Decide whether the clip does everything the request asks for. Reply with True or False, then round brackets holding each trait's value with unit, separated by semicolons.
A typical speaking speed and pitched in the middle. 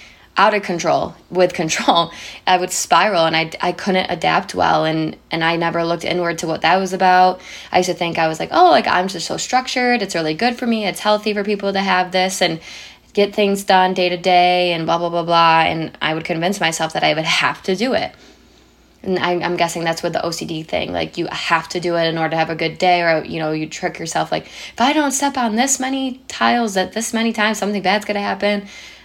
False (245 wpm; 180 Hz)